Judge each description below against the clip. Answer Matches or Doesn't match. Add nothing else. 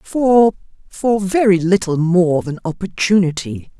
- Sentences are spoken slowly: Matches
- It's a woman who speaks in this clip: Matches